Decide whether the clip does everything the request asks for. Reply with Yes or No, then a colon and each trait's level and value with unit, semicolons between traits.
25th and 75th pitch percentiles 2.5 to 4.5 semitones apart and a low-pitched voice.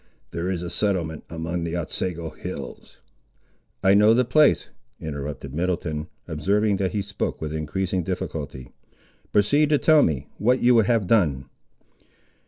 No: average, 4.9 semitones; very low, 90 Hz